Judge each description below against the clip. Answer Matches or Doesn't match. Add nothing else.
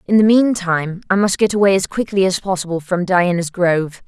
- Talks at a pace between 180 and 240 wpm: Matches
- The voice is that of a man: Doesn't match